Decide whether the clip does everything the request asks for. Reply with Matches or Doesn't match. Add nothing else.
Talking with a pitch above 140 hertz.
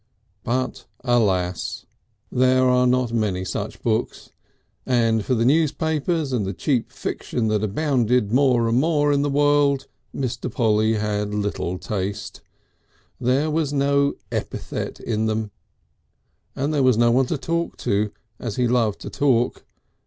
Doesn't match